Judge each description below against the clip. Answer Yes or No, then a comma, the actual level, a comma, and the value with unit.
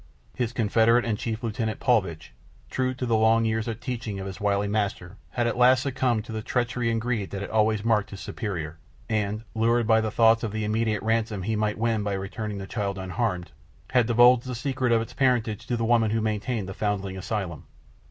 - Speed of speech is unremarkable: No, fast, 215 wpm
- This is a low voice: Yes, low, 110 Hz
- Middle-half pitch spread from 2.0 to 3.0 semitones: Yes, narrow, 2.4 semitones